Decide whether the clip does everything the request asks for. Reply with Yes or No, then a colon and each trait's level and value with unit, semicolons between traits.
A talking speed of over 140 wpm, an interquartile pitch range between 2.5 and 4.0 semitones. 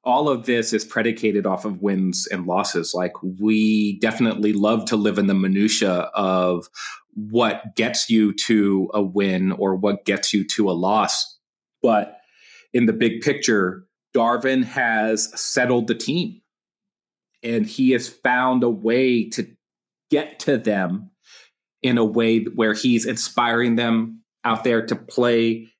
Yes: average, 150 wpm; average, 2.8 semitones